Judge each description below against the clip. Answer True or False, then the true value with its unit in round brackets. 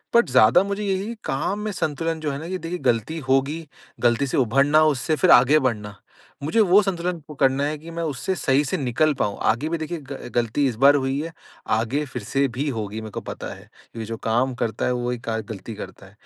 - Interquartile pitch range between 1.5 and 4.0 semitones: False (5.2 semitones)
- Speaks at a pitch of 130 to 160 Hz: True (140 Hz)